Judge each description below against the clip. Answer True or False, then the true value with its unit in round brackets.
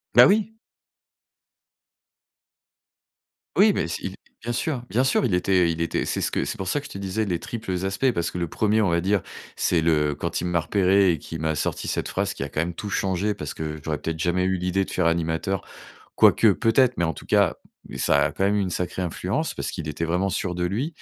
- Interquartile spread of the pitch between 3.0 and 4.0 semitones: True (3.6 semitones)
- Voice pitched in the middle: False (90 Hz)